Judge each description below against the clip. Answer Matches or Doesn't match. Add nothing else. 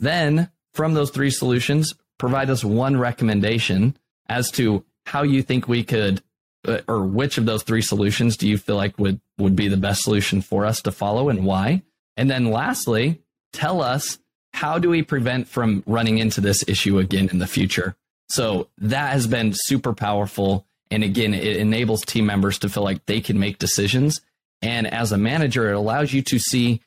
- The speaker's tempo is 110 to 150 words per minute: Doesn't match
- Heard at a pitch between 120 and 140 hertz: Doesn't match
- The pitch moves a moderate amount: Matches